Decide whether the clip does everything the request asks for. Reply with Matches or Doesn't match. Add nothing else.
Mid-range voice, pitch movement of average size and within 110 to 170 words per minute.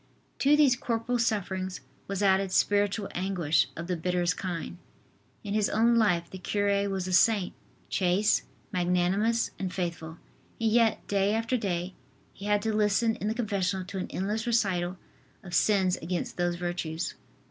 Doesn't match